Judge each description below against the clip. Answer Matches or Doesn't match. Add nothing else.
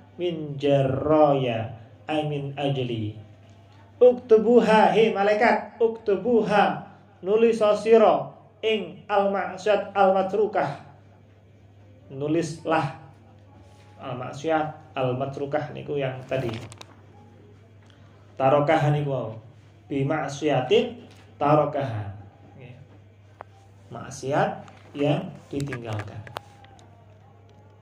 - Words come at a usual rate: Doesn't match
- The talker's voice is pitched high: Doesn't match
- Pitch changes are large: Matches